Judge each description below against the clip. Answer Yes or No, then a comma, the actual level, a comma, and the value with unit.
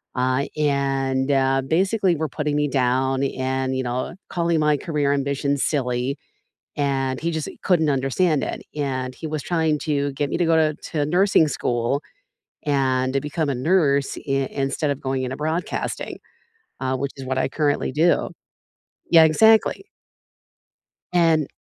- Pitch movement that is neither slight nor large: Yes, average, 3.0 semitones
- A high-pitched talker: No, medium, 140 Hz